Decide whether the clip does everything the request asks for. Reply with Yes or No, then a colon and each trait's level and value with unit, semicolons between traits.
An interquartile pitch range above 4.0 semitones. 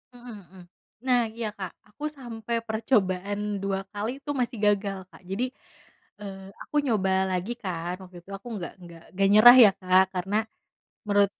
No: average, 3.4 semitones